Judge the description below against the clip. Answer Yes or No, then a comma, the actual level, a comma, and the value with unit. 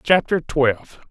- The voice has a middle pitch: Yes, medium, 145 Hz